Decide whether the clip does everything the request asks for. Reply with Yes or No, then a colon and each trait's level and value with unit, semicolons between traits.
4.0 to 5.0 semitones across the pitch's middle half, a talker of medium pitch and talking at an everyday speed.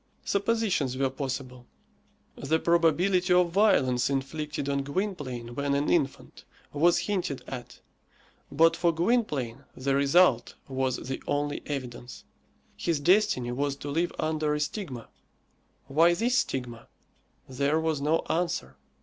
No: average, 4.5 semitones; medium, 145 Hz; slow, 125 wpm